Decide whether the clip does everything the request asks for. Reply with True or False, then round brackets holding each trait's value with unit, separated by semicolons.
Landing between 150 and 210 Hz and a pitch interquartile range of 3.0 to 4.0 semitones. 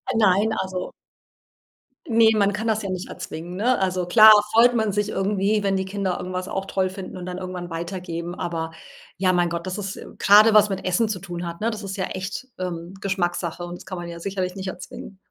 False (190 Hz; 2.4 semitones)